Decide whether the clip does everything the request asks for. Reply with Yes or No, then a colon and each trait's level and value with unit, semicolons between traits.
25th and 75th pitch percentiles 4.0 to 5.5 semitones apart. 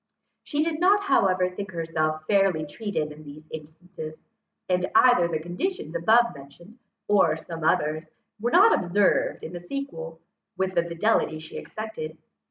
Yes: average, 5.2 semitones